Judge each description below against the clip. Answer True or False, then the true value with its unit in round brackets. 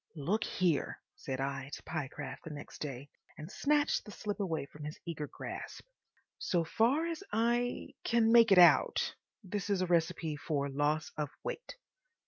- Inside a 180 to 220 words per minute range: False (155 wpm)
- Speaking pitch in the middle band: True (170 Hz)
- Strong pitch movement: True (6.7 semitones)